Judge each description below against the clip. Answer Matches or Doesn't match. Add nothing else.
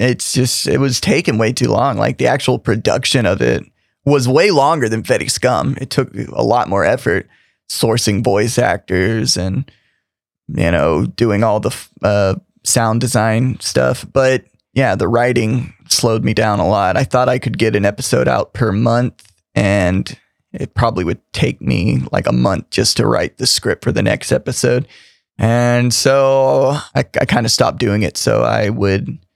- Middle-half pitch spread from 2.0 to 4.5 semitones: Matches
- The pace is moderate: Matches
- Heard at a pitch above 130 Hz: Doesn't match